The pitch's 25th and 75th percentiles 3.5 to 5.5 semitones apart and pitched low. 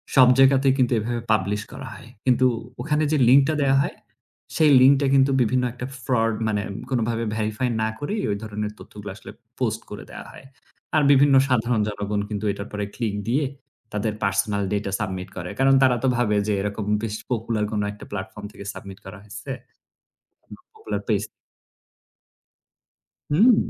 Yes: average, 4.4 semitones; low, 115 Hz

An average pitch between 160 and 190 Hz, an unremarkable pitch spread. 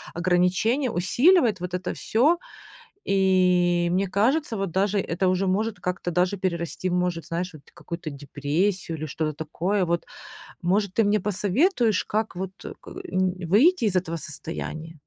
Yes: medium, 185 Hz; average, 3.3 semitones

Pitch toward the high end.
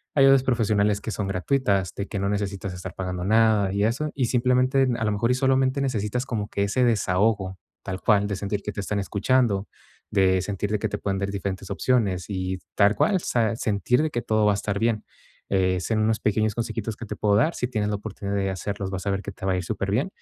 No: low, 105 Hz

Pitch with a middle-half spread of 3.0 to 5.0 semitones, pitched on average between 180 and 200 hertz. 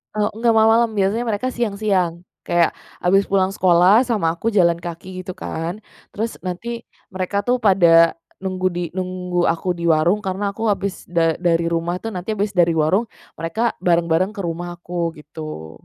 Yes: average, 3.4 semitones; medium, 185 Hz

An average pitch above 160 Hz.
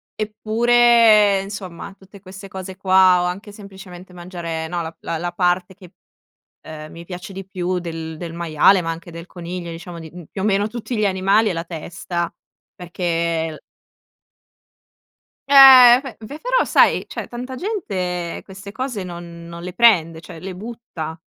Yes: medium, 185 Hz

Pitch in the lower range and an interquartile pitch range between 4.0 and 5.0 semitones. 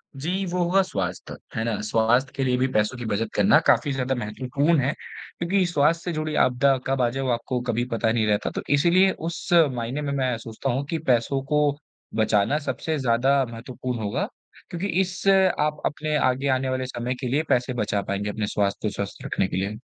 Yes: low, 130 Hz; average, 4.5 semitones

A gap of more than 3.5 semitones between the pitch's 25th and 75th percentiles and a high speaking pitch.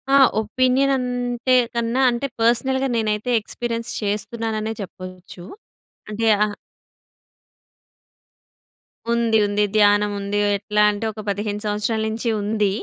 No: narrow, 2.4 semitones; high, 220 Hz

